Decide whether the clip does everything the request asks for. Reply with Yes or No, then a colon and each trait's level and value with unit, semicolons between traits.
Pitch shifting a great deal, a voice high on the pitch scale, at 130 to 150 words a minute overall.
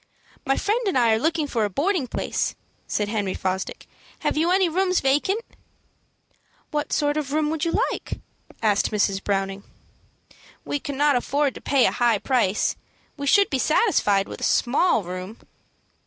No: wide, 6.9 semitones; very high, 270 Hz; average, 170 wpm